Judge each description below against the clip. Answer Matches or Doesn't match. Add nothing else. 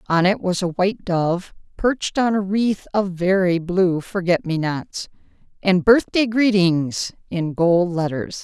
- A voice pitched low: Doesn't match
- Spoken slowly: Doesn't match